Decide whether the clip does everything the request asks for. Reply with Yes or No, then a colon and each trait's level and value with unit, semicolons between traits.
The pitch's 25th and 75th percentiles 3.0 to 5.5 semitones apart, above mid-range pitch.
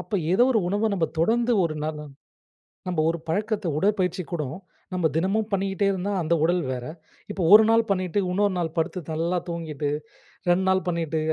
No: average, 3.6 semitones; medium, 180 Hz